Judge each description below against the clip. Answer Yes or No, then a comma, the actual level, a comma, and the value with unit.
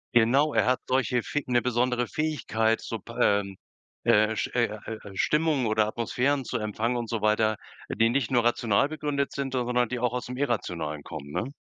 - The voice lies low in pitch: Yes, low, 120 Hz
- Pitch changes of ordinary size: Yes, average, 3.0 semitones